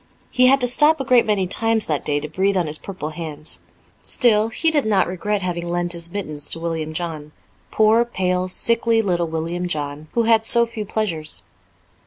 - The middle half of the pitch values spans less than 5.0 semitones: No, wide, 5.6 semitones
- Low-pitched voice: No, medium, 185 Hz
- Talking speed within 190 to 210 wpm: Yes, average, 195 wpm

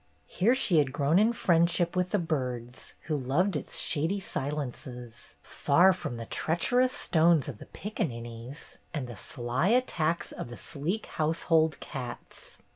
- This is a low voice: No, medium, 155 Hz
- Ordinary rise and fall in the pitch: No, wide, 6.0 semitones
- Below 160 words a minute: Yes, average, 145 wpm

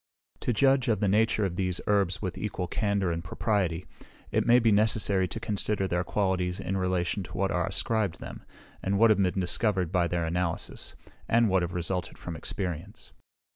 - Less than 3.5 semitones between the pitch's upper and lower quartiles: Yes, average, 2.9 semitones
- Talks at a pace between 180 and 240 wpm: Yes, average, 185 wpm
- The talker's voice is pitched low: Yes, very low, 95 Hz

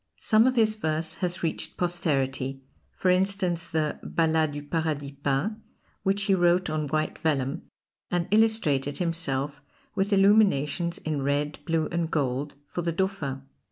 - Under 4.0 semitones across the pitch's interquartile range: No, average, 4.3 semitones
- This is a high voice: No, medium, 165 Hz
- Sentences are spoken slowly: No, average, 145 wpm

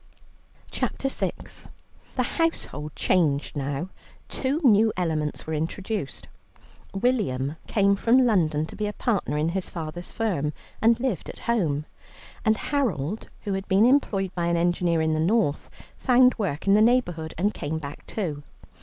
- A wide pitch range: Yes, wide, 6.2 semitones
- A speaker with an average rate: Yes, average, 155 wpm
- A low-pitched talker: No, medium, 185 Hz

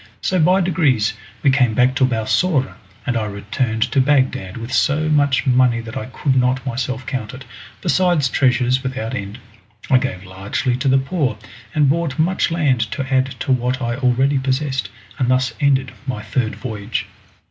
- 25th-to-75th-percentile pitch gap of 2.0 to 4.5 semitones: Yes, narrow, 2.5 semitones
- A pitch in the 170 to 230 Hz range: No, low, 130 Hz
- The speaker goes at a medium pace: Yes, average, 175 wpm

